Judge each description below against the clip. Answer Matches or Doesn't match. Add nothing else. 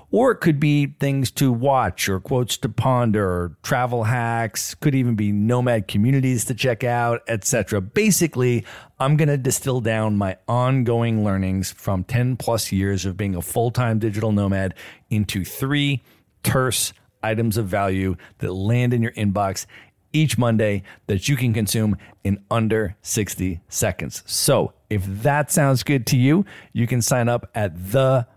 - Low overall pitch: Matches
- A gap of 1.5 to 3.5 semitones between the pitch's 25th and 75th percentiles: Doesn't match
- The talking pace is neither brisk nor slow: Matches